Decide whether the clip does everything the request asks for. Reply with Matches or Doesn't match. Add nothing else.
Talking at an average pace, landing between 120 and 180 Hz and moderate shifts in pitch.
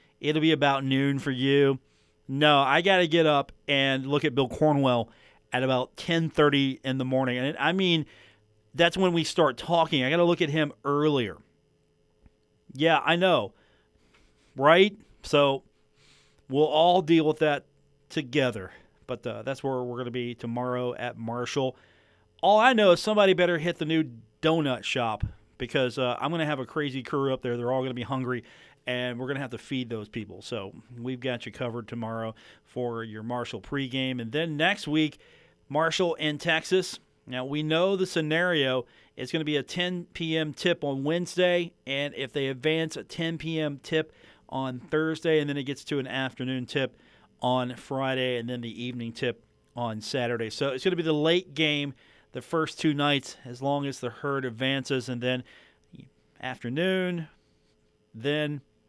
Matches